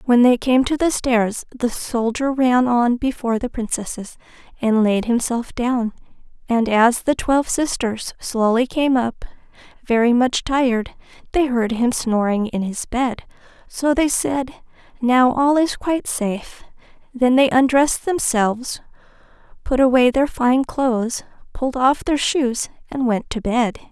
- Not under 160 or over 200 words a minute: No, average, 150 wpm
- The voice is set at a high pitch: Yes, high, 245 Hz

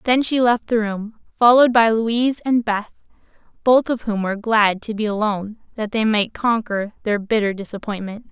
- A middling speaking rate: Yes, average, 180 wpm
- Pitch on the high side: Yes, high, 220 Hz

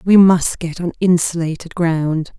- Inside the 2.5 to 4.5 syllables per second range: Yes, 4.1 syllables/s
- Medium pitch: Yes, medium, 170 Hz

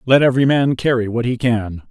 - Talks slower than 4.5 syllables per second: No, 5.8 syllables/s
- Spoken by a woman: No, male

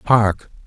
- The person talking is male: Yes, male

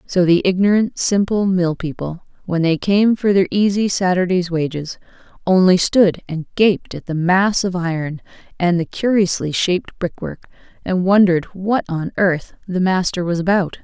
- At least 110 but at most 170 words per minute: Yes, average, 160 wpm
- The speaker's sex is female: Yes, female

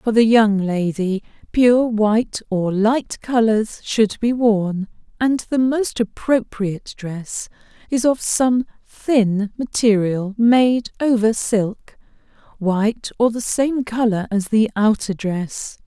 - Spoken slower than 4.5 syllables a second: Yes, 3.4 syllables/s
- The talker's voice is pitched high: Yes, high, 220 Hz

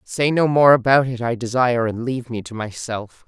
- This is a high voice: No, low, 125 Hz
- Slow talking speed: No, fast, 220 wpm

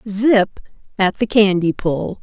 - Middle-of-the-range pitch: No, high, 200 Hz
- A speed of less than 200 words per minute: Yes, slow, 135 wpm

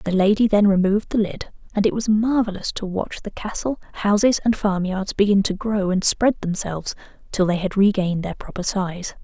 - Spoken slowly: No, average, 195 wpm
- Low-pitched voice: No, high, 200 Hz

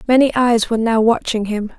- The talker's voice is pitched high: Yes, high, 230 Hz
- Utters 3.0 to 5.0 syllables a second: No, 5.6 syllables/s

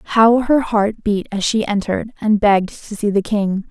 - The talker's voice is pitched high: Yes, high, 210 Hz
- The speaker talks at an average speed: No, fast, 210 wpm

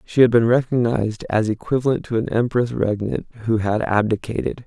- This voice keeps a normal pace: Yes, average, 165 wpm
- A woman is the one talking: No, male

